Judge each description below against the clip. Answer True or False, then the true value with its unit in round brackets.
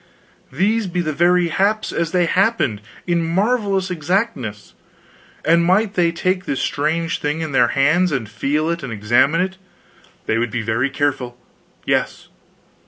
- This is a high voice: False (165 Hz)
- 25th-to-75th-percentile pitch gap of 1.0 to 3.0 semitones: False (5.3 semitones)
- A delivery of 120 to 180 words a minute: True (160 wpm)